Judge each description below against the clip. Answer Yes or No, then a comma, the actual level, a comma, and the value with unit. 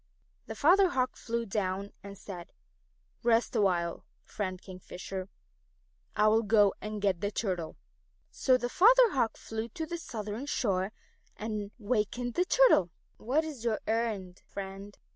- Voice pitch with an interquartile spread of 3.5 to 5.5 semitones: Yes, average, 3.9 semitones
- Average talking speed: Yes, average, 145 wpm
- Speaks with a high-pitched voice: Yes, high, 215 Hz